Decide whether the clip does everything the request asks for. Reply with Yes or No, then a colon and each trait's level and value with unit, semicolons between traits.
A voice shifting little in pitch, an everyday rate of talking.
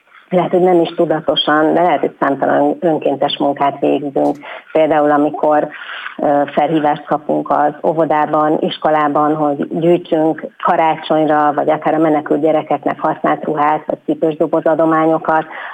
Yes: narrow, 1.4 semitones; average, 120 wpm